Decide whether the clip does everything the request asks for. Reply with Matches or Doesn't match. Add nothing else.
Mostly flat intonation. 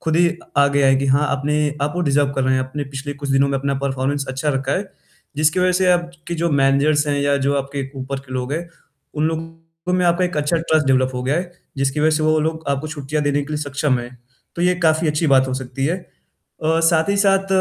Doesn't match